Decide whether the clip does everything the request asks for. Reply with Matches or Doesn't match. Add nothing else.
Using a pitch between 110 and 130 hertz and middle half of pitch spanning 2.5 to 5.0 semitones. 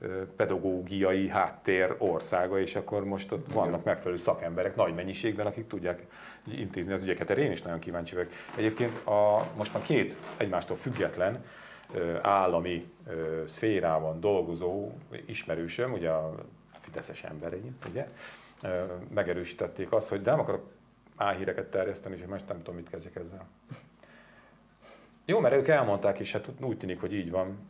Doesn't match